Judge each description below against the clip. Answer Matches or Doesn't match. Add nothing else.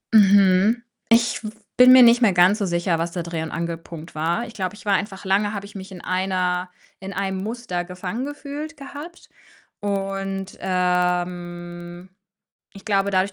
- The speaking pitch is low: Doesn't match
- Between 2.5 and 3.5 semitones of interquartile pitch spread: Matches